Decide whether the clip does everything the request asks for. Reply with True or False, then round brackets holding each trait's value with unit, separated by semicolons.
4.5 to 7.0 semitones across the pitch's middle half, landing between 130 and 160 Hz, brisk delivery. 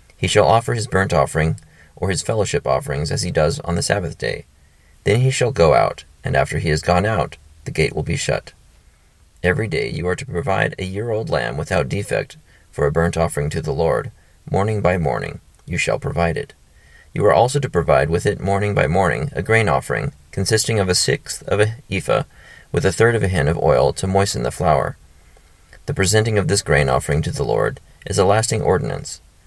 False (4.9 semitones; 90 Hz; 210 wpm)